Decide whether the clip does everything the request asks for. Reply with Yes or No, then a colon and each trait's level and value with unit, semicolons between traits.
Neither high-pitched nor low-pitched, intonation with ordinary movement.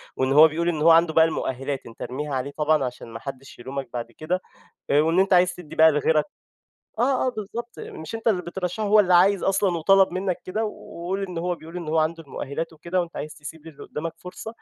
Yes: medium, 165 Hz; average, 3.6 semitones